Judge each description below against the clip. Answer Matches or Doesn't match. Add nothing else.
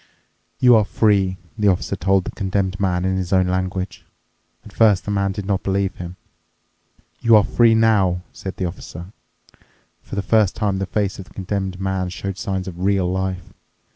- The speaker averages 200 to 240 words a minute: Doesn't match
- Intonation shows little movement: Matches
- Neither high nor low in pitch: Doesn't match